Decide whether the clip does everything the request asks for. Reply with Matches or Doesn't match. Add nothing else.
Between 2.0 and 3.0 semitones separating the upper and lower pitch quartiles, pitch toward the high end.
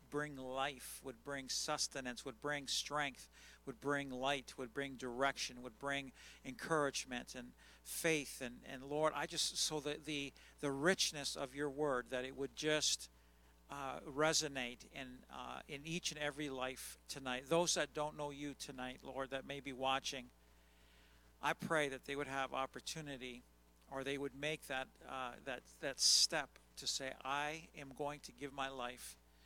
Doesn't match